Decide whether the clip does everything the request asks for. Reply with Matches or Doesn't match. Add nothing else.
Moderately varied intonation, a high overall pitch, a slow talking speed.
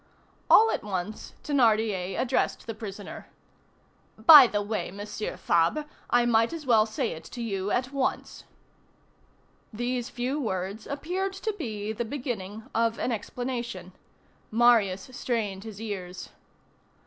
Matches